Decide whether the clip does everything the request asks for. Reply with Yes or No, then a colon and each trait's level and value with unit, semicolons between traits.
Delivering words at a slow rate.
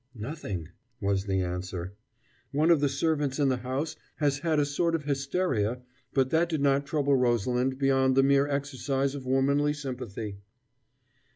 No: average, 160 wpm